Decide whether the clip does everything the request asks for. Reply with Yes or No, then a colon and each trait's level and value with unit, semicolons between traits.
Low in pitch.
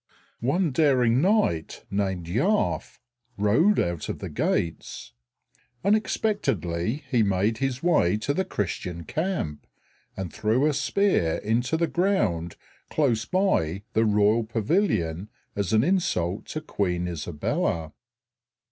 Yes: low, 110 Hz